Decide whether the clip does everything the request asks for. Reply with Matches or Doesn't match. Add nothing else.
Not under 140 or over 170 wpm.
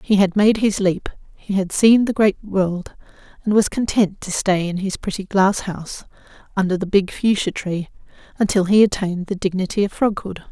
Doesn't match